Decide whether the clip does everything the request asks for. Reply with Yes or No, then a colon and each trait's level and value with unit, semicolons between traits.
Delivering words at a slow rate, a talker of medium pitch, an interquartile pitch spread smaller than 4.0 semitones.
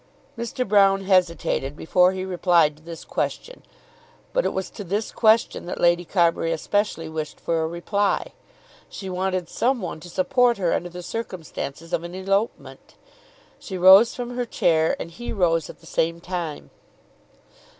No: average, 160 wpm; medium, 180 Hz; average, 3.4 semitones